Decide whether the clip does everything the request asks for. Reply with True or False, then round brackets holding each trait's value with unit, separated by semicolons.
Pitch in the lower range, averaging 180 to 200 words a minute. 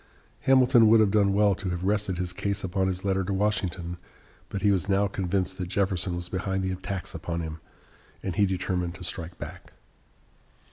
True (95 Hz; 190 wpm)